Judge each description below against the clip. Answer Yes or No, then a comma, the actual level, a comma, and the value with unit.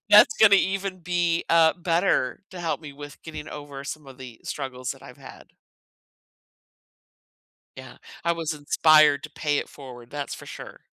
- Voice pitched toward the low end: No, medium, 155 Hz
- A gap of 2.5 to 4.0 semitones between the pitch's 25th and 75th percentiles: Yes, average, 3.5 semitones